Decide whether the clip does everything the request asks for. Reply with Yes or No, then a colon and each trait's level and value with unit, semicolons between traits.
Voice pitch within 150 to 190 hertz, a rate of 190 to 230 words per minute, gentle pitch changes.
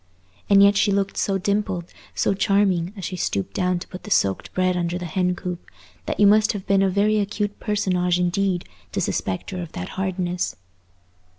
Yes: medium, 185 Hz; average, 195 wpm; narrow, 2.1 semitones